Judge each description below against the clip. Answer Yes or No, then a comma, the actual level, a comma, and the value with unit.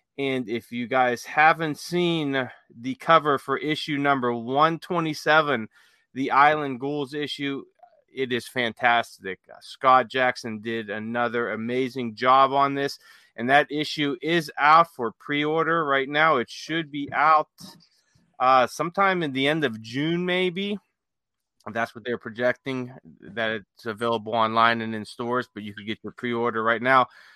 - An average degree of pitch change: Yes, average, 4.4 semitones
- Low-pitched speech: Yes, low, 130 Hz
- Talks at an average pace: Yes, average, 145 wpm